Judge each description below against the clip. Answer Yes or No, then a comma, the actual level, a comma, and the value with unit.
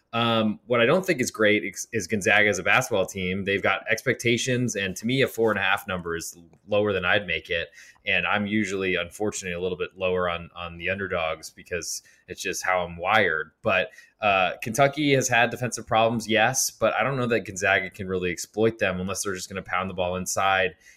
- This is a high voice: No, low, 100 Hz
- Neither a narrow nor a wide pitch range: Yes, average, 3.5 semitones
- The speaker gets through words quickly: Yes, fast, 220 wpm